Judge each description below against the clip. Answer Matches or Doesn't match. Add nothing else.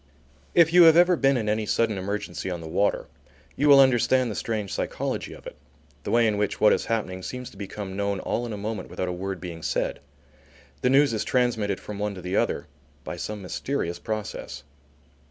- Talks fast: Matches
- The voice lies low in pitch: Matches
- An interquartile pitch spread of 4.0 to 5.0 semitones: Matches